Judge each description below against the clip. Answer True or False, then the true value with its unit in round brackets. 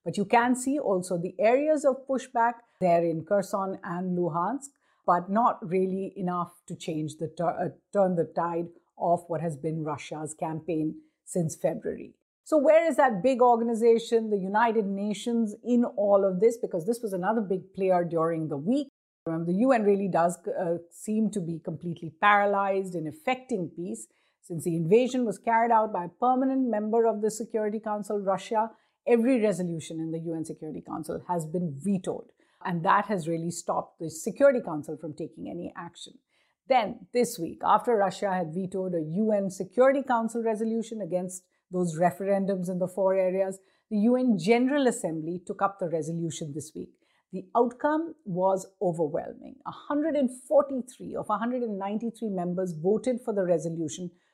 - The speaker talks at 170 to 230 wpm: False (160 wpm)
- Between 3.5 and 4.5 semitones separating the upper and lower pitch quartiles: False (5.0 semitones)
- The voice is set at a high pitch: True (195 Hz)